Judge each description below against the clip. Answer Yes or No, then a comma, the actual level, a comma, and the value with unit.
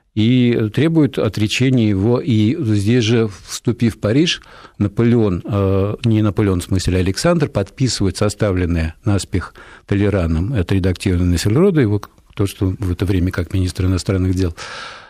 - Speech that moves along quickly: No, average, 140 wpm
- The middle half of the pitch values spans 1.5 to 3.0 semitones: No, average, 3.7 semitones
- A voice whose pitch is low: Yes, low, 105 Hz